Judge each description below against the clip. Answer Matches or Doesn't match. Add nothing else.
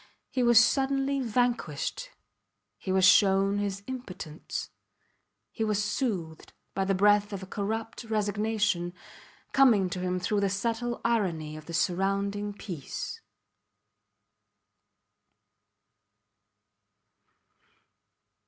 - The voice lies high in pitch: Matches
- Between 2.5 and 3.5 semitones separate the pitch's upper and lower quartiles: Matches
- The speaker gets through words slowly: Matches